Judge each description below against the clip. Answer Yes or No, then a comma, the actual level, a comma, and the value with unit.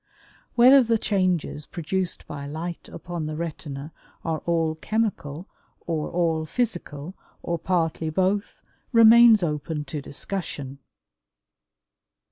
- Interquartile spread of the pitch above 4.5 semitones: No, average, 3.9 semitones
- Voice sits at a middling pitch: Yes, medium, 170 Hz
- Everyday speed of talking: No, slow, 105 wpm